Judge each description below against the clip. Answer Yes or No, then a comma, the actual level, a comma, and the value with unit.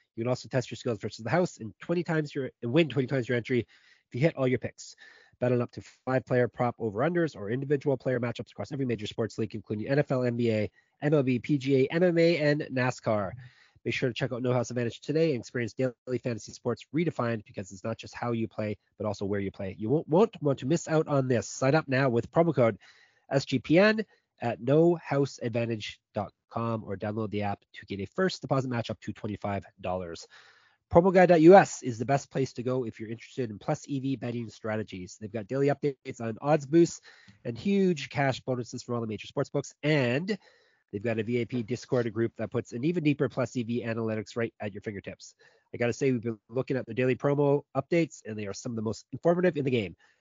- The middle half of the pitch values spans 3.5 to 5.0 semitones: Yes, average, 3.8 semitones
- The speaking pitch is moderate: No, low, 125 Hz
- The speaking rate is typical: No, fast, 215 wpm